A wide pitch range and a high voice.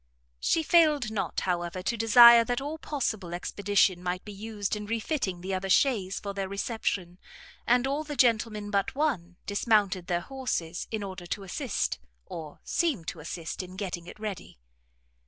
No: average, 4.5 semitones; high, 205 Hz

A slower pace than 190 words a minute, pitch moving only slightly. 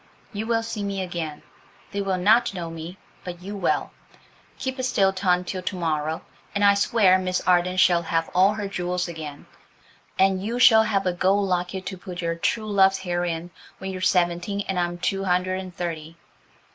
No: average, 195 wpm; narrow, 2.3 semitones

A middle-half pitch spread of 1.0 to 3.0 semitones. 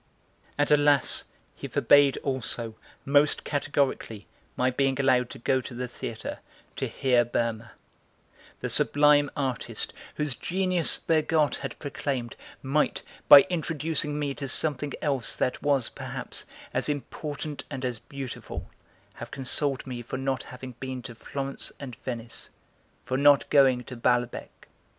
Yes: narrow, 2.5 semitones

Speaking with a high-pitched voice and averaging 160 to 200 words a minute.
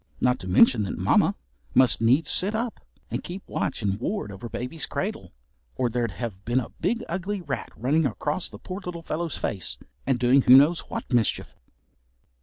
No: low, 130 Hz; average, 185 wpm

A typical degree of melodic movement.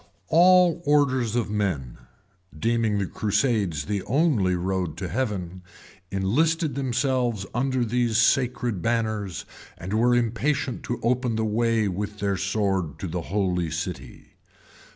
Yes: average, 4.6 semitones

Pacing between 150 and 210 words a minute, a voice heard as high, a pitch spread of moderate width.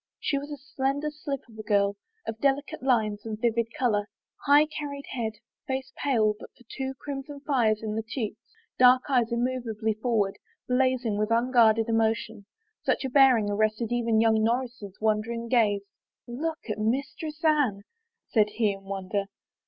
Yes: average, 165 wpm; high, 235 Hz; average, 3.6 semitones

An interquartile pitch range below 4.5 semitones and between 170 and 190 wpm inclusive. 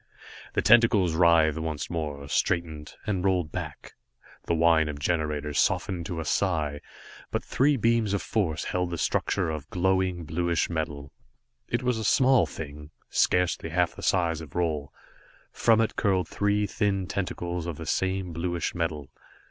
No: average, 3.3 semitones; average, 160 wpm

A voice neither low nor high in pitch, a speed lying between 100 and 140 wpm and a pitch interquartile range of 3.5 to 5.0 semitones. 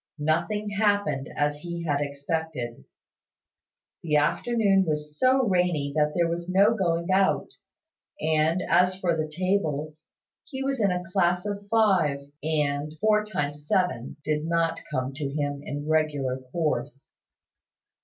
Yes: medium, 165 Hz; slow, 135 wpm; average, 4.3 semitones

